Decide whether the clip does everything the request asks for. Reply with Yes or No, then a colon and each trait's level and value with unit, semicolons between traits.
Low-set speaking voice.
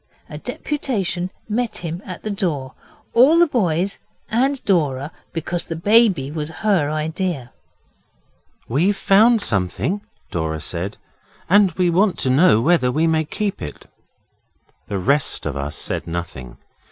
No: medium, 165 Hz